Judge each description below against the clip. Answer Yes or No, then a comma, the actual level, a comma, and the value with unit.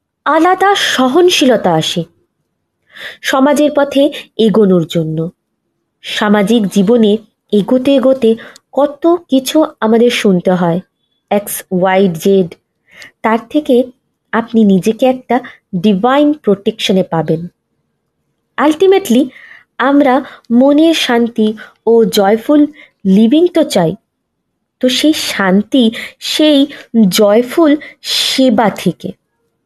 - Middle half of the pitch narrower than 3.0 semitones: No, wide, 5.6 semitones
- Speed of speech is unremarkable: Yes, average, 85 wpm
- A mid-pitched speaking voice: No, high, 235 Hz